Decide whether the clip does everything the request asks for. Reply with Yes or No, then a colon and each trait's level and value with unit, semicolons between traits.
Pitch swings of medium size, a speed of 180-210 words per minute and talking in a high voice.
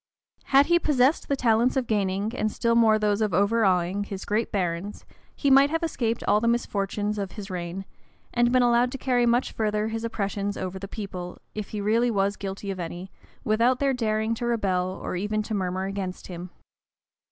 Yes: average, 3.5 semitones; average, 195 wpm; high, 215 Hz